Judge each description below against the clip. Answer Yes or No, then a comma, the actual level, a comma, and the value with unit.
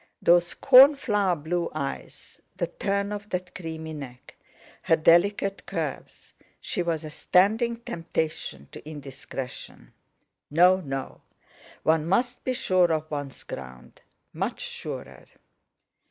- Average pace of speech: No, slow, 110 wpm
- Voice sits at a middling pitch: Yes, medium, 170 Hz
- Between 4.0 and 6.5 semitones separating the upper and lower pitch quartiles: Yes, average, 4.5 semitones